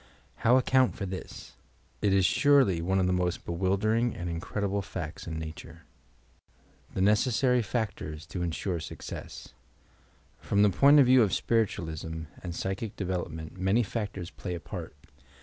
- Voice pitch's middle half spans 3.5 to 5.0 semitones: Yes, average, 4.3 semitones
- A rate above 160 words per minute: No, average, 155 wpm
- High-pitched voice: No, very low, 95 Hz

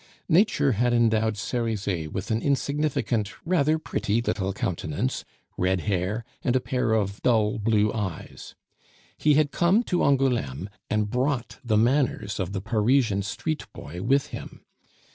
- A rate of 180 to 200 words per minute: No, average, 145 wpm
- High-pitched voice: No, low, 115 Hz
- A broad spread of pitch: No, average, 5.0 semitones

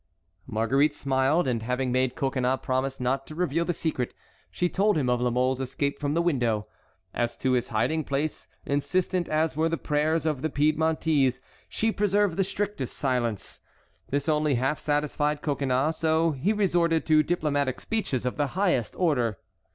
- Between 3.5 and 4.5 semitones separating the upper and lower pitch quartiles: Yes, average, 3.9 semitones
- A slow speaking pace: No, average, 165 wpm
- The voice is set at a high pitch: No, medium, 145 Hz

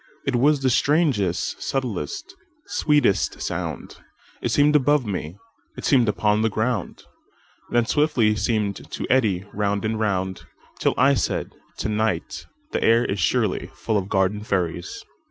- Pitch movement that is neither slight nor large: Yes, average, 4.9 semitones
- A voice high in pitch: No, low, 110 Hz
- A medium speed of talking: No, slow, 125 wpm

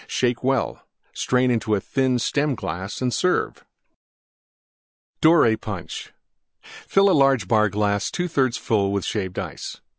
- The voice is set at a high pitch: No, low, 120 Hz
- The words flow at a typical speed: No, slow, 115 wpm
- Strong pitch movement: No, average, 4.8 semitones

